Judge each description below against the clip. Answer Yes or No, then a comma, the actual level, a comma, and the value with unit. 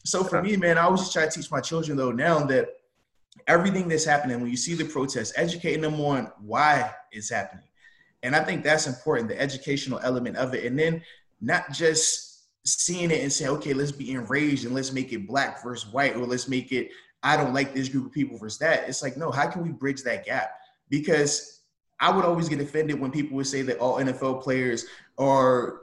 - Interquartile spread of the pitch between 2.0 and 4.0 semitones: Yes, average, 3.6 semitones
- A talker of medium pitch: Yes, medium, 145 Hz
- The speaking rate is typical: No, fast, 220 wpm